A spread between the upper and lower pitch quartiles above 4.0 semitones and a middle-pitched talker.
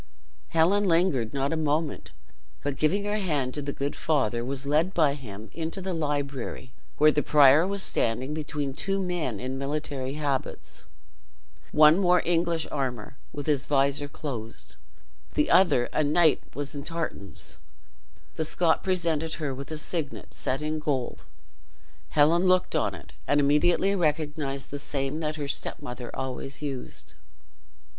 No: average, 3.0 semitones; medium, 150 Hz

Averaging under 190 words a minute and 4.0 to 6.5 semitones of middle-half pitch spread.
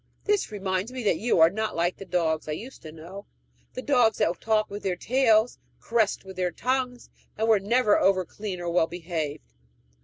No: average, 195 wpm; average, 4.5 semitones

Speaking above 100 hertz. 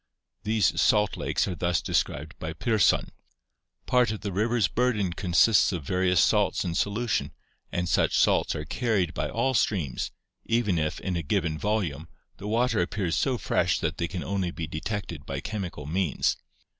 No: very low, 95 Hz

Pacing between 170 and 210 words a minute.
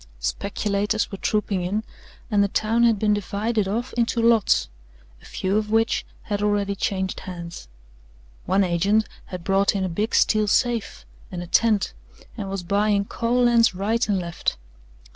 No: average, 160 wpm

